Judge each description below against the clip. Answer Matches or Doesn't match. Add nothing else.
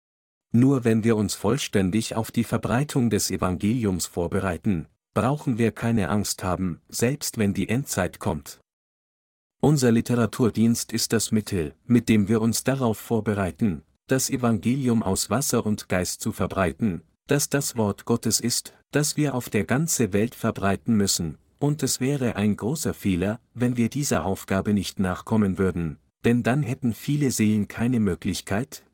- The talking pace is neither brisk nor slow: Matches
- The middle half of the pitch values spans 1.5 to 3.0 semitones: Doesn't match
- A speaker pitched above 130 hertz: Doesn't match